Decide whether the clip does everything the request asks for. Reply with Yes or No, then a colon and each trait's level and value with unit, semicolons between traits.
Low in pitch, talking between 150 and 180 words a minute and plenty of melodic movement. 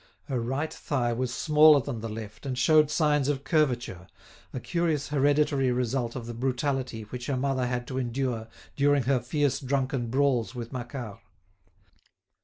No: low, 130 Hz; average, 160 wpm; average, 2.9 semitones